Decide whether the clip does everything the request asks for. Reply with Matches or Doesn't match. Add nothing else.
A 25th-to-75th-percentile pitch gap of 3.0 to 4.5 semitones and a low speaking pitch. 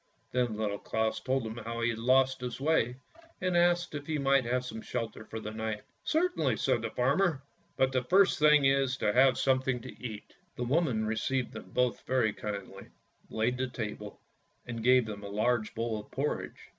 Matches